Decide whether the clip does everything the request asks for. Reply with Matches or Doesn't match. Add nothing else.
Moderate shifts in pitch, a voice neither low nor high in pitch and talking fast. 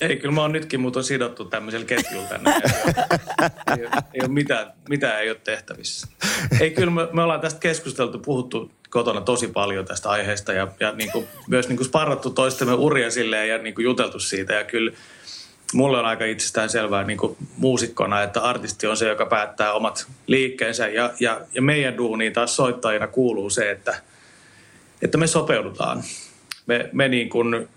Doesn't match